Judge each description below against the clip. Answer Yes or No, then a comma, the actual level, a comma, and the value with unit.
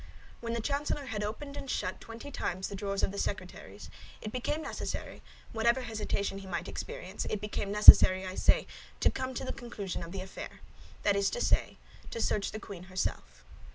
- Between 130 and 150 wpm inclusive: No, average, 190 wpm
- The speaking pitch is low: No, high, 210 Hz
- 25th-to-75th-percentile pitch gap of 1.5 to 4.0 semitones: Yes, average, 3.5 semitones